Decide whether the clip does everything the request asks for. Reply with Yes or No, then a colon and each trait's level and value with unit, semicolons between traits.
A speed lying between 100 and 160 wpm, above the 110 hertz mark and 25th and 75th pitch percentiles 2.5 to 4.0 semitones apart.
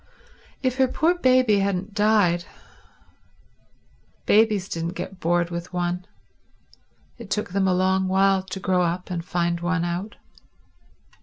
Yes: slow, 135 wpm; medium, 185 Hz; average, 2.9 semitones